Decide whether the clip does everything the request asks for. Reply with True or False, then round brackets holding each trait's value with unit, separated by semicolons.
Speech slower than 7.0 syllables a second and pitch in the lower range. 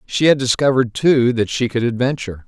True (6.0 syllables/s; 125 Hz)